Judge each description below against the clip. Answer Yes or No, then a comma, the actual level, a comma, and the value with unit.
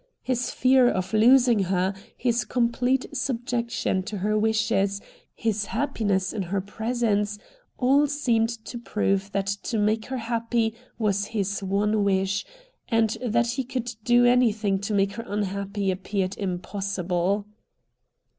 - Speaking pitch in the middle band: No, high, 215 Hz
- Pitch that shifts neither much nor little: Yes, average, 3.3 semitones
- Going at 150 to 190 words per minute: No, slow, 135 wpm